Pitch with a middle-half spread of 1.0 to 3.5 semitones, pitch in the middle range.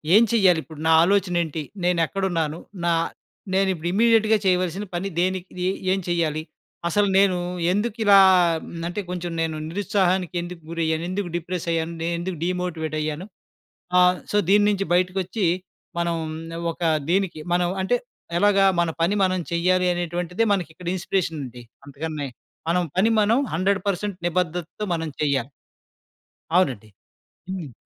Yes: narrow, 2.6 semitones; medium, 180 Hz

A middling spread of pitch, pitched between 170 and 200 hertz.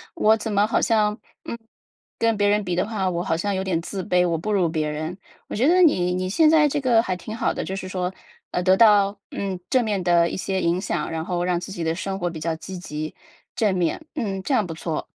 Yes: average, 3.4 semitones; high, 190 Hz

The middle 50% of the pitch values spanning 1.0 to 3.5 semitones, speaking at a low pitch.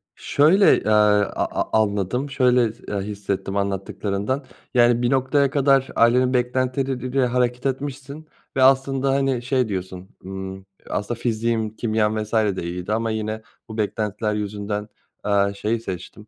No: average, 4.1 semitones; low, 115 Hz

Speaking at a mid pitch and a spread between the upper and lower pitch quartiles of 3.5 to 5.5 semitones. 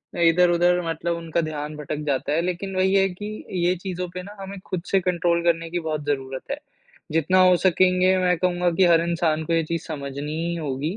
No: medium, 170 Hz; narrow, 2.5 semitones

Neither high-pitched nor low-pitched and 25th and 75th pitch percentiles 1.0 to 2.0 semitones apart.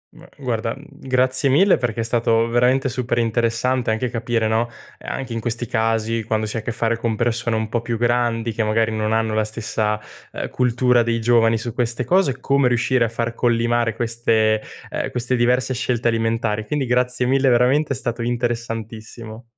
No: low, 115 Hz; narrow, 1.7 semitones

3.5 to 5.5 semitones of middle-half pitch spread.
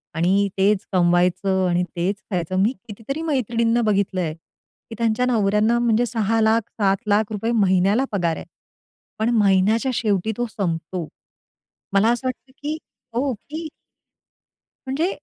Yes: average, 3.9 semitones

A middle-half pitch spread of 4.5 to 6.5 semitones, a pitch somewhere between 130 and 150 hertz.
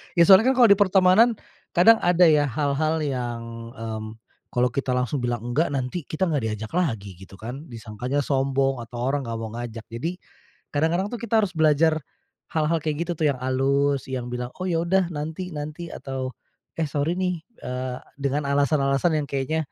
Yes: average, 5.0 semitones; medium, 140 Hz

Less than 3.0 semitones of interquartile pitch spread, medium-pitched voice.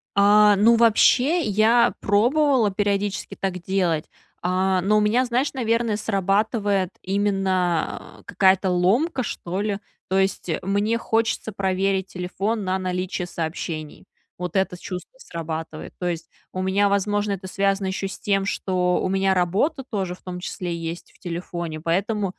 No: narrow, 2.6 semitones; high, 195 Hz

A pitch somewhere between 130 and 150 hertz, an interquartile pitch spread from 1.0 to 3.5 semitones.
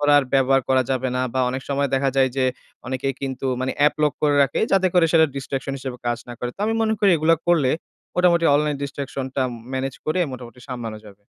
Yes: low, 135 Hz; narrow, 2.4 semitones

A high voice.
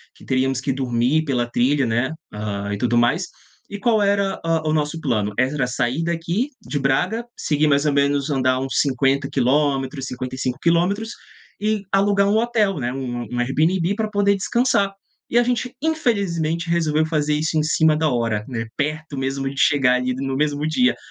No: medium, 150 Hz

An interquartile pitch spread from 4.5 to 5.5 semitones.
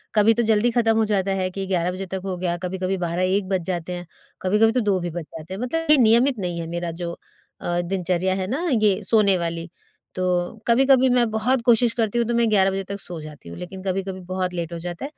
No: average, 4.0 semitones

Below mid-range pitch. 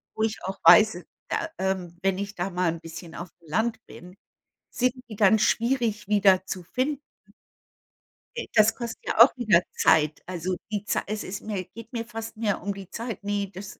No: high, 200 Hz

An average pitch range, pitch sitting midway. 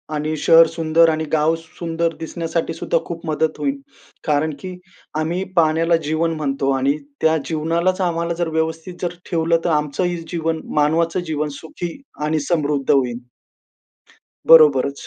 No: narrow, 1.5 semitones; medium, 160 Hz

